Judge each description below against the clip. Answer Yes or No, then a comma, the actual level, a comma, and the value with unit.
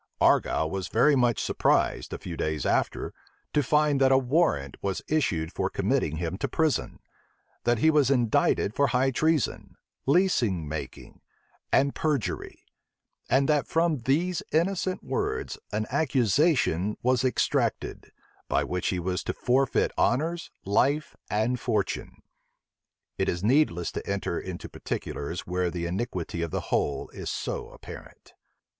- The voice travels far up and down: Yes, wide, 8.4 semitones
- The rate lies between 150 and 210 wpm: No, average, 140 wpm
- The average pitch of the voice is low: Yes, low, 125 Hz